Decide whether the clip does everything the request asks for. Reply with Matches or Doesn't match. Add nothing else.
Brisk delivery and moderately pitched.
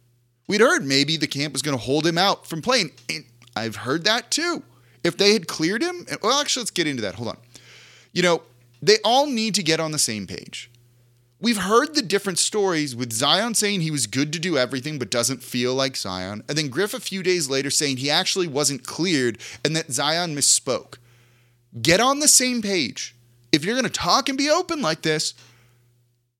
Matches